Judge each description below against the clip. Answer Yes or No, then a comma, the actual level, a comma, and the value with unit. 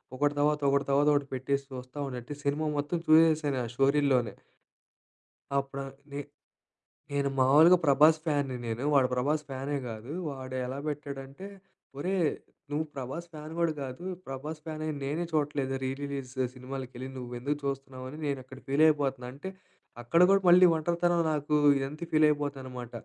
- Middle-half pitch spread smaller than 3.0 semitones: Yes, narrow, 2.5 semitones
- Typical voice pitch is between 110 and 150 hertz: Yes, medium, 140 Hz